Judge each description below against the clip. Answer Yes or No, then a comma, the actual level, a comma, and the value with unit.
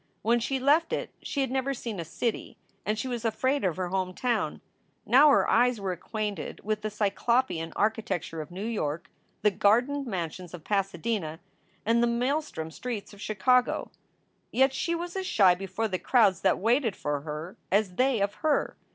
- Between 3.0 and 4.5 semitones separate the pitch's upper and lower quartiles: No, average, 5.2 semitones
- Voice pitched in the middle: No, high, 215 Hz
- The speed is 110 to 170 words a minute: No, average, 180 wpm